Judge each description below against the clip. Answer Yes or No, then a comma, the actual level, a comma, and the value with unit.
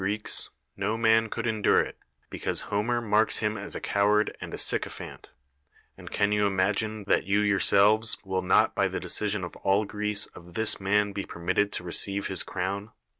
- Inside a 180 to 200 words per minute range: Yes, average, 185 wpm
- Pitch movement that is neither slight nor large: No, narrow, 1.6 semitones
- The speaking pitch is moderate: No, low, 105 Hz